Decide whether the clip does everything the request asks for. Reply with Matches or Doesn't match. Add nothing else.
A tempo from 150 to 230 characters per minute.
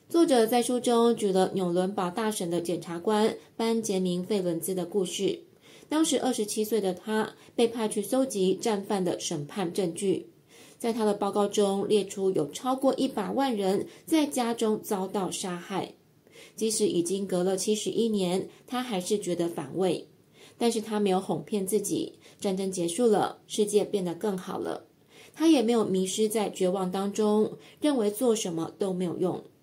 Doesn't match